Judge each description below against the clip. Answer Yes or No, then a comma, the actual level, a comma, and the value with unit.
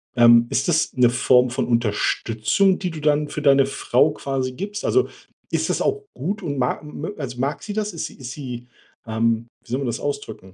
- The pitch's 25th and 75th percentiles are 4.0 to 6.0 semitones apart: Yes, average, 4.5 semitones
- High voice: No, low, 135 Hz